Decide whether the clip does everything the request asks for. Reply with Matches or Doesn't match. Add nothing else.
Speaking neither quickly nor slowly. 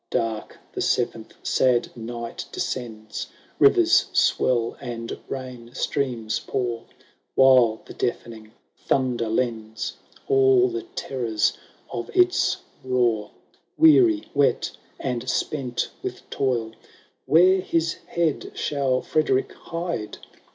Doesn't match